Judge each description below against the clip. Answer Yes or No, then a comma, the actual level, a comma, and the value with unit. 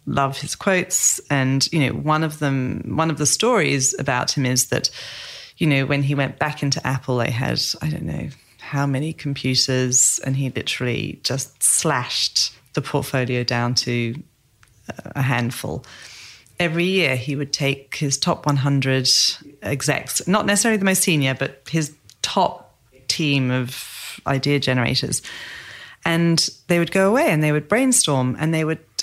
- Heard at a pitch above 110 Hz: Yes, medium, 140 Hz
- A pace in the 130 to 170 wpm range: Yes, average, 160 wpm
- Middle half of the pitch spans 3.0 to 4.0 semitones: Yes, average, 3.4 semitones